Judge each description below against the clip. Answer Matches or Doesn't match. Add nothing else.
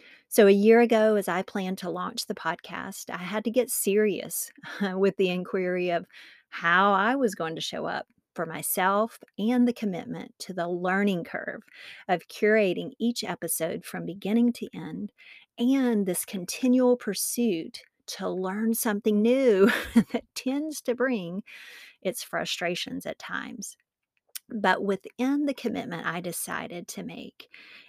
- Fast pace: Doesn't match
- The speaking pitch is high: Matches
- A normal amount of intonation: Matches